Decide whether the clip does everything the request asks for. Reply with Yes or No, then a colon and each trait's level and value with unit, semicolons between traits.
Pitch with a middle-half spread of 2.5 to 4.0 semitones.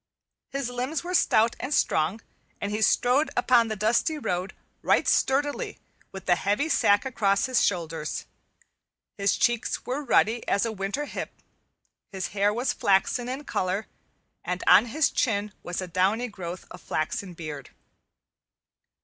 No: average, 5.0 semitones